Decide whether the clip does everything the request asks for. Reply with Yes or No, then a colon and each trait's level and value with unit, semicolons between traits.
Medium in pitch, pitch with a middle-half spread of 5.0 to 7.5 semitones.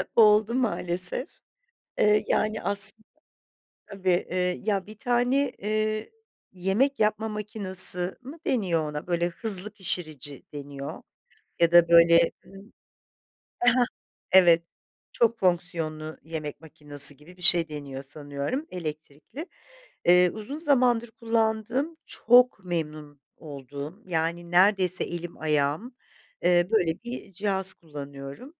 Yes: medium, 180 Hz; average, 5.3 semitones